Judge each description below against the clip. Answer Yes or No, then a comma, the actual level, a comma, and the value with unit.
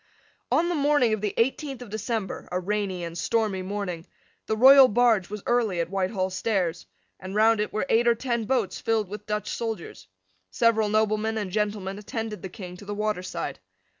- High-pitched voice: Yes, high, 210 Hz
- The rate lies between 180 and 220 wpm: Yes, average, 185 wpm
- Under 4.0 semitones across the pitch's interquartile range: Yes, average, 3.0 semitones